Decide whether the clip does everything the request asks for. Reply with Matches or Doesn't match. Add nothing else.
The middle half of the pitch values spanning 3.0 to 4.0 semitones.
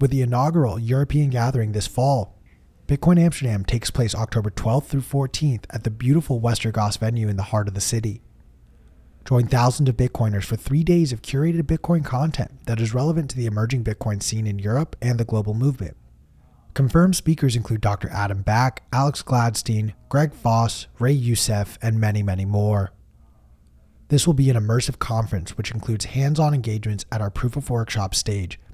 Doesn't match